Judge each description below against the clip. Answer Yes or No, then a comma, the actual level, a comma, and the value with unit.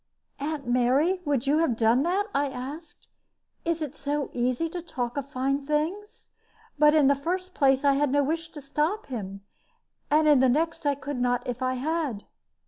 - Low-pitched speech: No, very high, 285 Hz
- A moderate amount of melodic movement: Yes, average, 3.6 semitones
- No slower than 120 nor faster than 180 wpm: No, average, 190 wpm